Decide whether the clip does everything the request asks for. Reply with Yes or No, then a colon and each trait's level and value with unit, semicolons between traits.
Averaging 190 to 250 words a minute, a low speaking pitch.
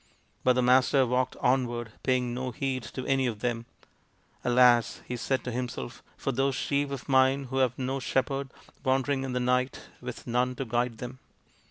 Yes: average, 195 wpm; low, 125 Hz